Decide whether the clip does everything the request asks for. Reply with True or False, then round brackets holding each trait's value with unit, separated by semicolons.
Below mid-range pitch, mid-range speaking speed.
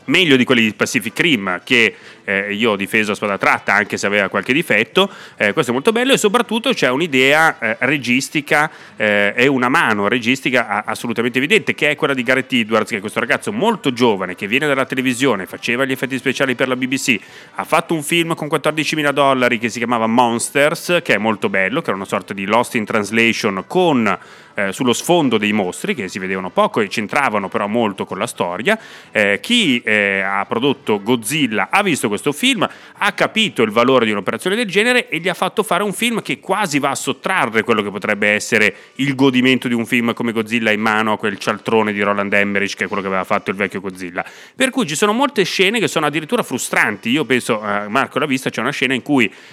False (130 Hz; 215 wpm)